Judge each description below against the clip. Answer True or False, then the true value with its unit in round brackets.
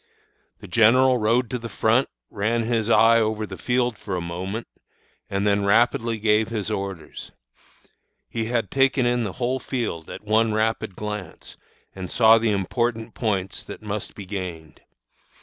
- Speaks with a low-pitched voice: True (110 Hz)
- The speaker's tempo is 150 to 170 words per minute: True (160 wpm)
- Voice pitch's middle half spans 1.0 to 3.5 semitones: True (2.7 semitones)